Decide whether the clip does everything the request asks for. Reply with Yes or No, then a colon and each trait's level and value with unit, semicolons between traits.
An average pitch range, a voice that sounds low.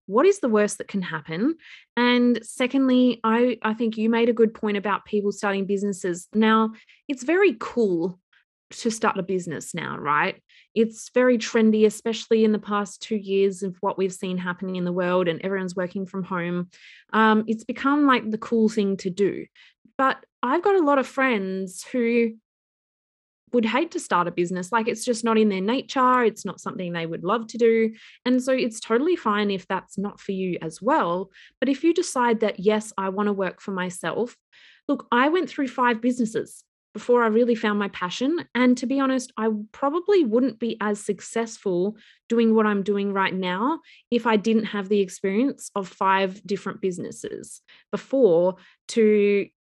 No: average, 3.8 semitones; high, 220 Hz